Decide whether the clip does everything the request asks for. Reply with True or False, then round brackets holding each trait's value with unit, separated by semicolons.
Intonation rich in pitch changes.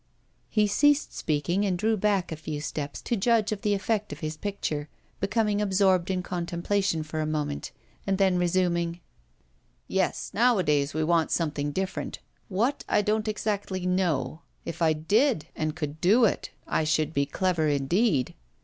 False (4.8 semitones)